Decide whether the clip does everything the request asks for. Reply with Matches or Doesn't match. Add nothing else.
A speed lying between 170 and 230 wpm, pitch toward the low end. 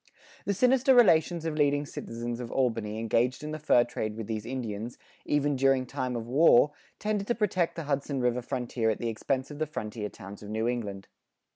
Matches